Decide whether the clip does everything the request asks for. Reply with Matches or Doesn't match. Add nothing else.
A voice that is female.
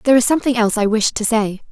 Matches